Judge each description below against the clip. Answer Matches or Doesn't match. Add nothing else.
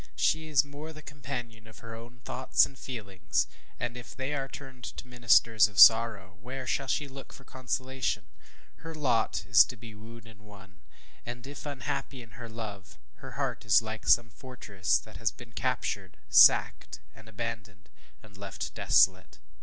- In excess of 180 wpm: Doesn't match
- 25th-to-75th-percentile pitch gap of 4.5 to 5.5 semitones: Doesn't match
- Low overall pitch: Matches